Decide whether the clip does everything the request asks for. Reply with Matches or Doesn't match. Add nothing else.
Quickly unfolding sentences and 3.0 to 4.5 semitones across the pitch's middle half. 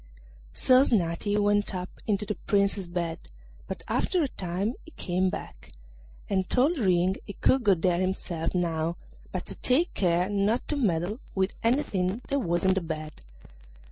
Doesn't match